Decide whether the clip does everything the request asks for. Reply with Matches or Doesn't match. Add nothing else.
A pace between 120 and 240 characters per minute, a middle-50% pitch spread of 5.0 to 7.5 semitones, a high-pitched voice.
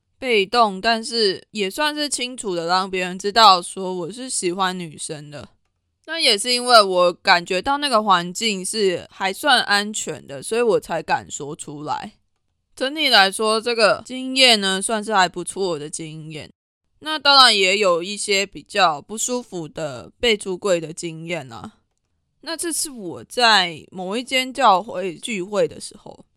Matches